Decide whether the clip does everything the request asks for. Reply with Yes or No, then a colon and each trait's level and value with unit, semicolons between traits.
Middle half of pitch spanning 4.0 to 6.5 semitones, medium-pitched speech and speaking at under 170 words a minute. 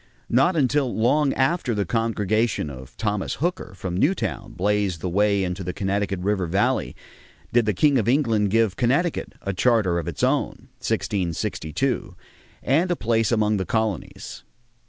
No: average, 4.7 semitones; low, 105 Hz; average, 155 wpm